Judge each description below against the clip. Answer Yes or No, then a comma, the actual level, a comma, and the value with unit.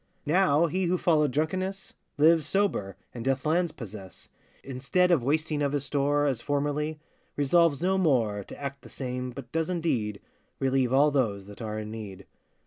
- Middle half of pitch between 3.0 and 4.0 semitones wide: No, average, 4.7 semitones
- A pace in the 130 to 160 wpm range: No, average, 170 wpm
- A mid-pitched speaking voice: Yes, medium, 145 Hz